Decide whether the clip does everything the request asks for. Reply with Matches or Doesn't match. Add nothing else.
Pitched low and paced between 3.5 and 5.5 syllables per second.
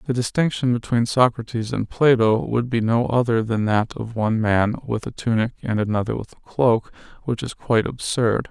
Matches